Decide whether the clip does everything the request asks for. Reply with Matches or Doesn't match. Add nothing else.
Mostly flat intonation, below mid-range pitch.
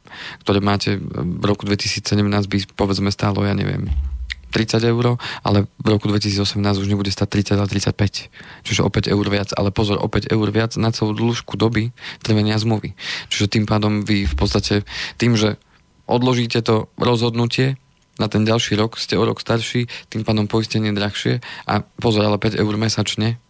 Matches